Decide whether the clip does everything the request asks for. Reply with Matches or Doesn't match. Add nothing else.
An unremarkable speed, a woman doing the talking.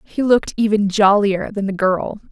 Matches